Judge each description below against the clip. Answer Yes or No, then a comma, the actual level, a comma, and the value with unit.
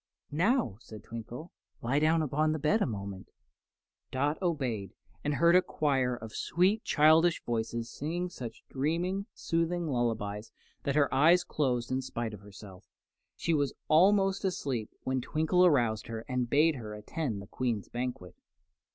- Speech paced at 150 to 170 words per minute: Yes, average, 155 wpm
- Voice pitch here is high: No, medium, 140 Hz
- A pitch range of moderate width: No, wide, 6.1 semitones